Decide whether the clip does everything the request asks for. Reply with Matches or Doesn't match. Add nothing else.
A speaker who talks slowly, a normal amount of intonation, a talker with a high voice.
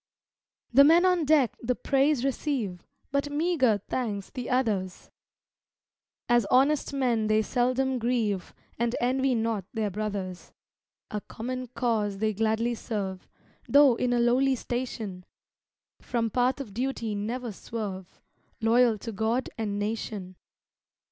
Matches